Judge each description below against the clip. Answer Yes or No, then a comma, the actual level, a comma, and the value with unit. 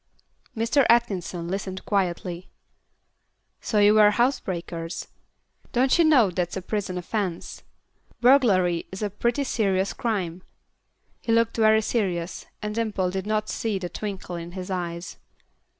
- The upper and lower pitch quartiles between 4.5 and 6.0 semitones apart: No, average, 3.8 semitones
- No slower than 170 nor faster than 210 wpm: No, slow, 135 wpm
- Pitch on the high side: Yes, high, 200 Hz